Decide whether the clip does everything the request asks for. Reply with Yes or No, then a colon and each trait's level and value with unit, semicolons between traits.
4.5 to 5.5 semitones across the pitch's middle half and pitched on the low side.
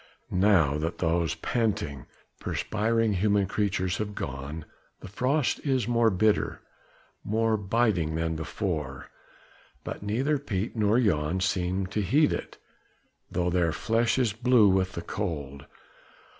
Yes: average, 5.0 semitones; low, 100 Hz